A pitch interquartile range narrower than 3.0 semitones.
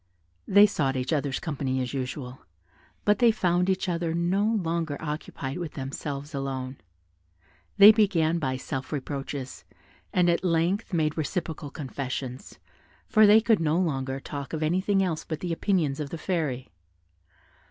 No: average, 4.8 semitones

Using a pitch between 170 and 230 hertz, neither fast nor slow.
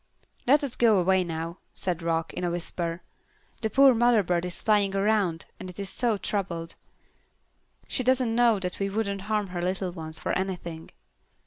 Yes: high, 190 Hz; average, 175 wpm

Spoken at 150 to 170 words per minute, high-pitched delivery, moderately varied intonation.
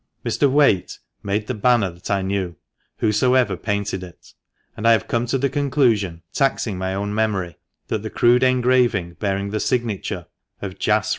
No: average, 165 wpm; low, 105 Hz; average, 4.3 semitones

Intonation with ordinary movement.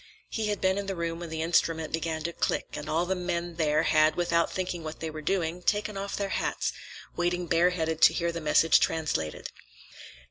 No: narrow, 1.9 semitones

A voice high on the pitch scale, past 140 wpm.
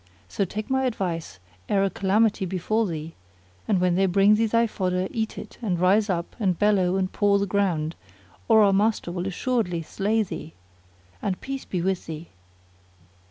Yes: high, 195 Hz; average, 175 wpm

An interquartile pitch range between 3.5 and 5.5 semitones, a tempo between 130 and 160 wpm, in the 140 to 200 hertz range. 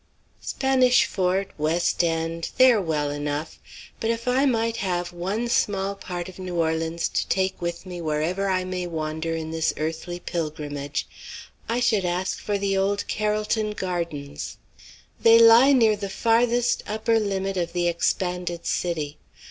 Yes: average, 4.4 semitones; average, 155 wpm; medium, 185 Hz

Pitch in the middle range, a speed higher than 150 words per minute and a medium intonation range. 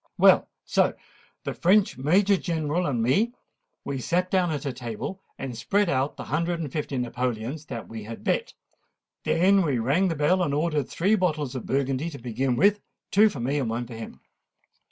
No: medium, 145 Hz; average, 180 wpm; wide, 6.1 semitones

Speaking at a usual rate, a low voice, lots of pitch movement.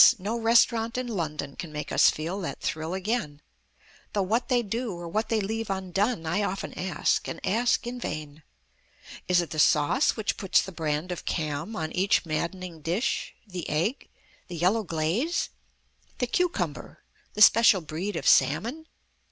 No: average, 160 wpm; high, 190 Hz; wide, 5.7 semitones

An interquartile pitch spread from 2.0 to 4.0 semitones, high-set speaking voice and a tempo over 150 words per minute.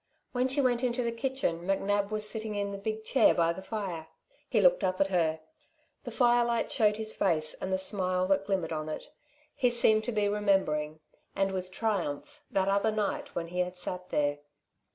Yes: average, 3.6 semitones; high, 200 Hz; average, 195 wpm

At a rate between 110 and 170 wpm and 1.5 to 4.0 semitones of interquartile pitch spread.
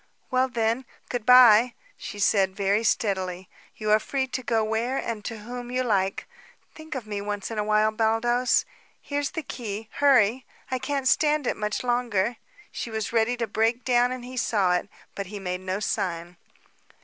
No: average, 185 wpm; average, 3.3 semitones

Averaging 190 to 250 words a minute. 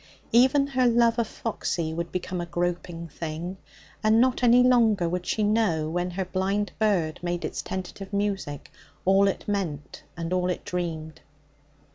No: average, 160 wpm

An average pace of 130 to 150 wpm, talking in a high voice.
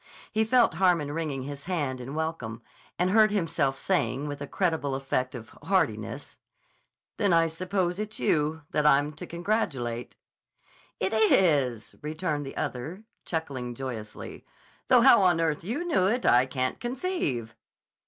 No: average, 145 wpm; medium, 160 Hz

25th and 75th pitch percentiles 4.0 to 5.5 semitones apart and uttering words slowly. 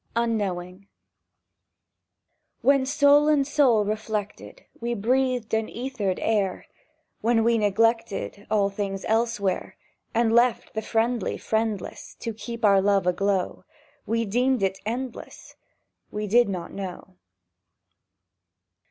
No: average, 3.1 semitones; slow, 110 wpm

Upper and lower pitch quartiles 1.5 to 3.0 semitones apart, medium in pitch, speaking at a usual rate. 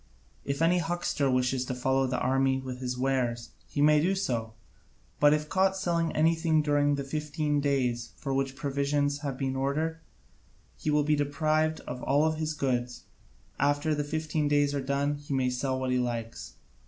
Yes: narrow, 2.6 semitones; medium, 145 Hz; average, 180 wpm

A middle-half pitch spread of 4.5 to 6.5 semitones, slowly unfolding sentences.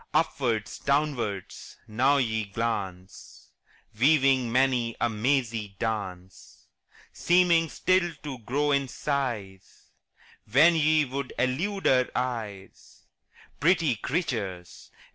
Yes: average, 5.1 semitones; slow, 95 wpm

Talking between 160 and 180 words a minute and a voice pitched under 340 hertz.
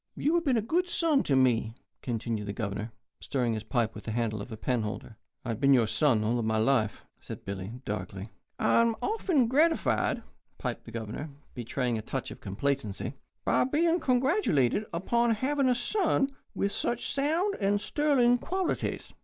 Yes: average, 170 wpm; medium, 140 Hz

